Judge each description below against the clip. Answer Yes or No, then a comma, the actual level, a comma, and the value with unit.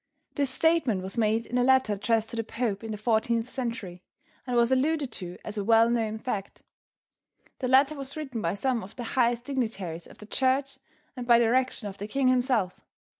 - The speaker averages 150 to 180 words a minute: No, average, 200 wpm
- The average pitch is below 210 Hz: No, high, 235 Hz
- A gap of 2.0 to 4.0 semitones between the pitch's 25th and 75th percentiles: Yes, average, 3.4 semitones